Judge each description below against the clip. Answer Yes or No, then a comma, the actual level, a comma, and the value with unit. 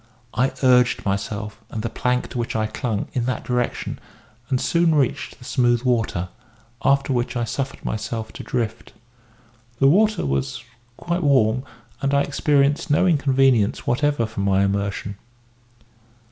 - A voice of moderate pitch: No, low, 125 Hz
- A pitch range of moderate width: Yes, average, 4.1 semitones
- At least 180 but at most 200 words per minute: No, average, 145 wpm